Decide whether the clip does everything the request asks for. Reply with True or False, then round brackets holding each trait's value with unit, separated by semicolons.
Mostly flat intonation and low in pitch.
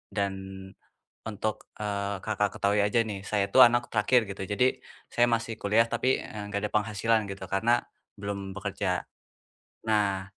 True (2.0 semitones; 105 Hz)